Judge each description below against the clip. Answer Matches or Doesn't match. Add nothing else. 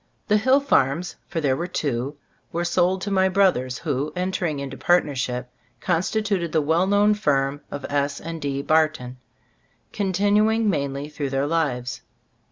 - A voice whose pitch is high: Doesn't match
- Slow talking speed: Doesn't match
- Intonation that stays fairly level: Doesn't match